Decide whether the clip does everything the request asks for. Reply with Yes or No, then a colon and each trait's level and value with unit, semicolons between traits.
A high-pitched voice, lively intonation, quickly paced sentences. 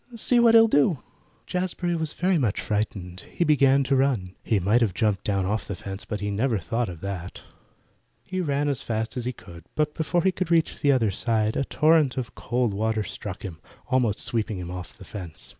No: low, 115 Hz; wide, 6.7 semitones; fast, 210 wpm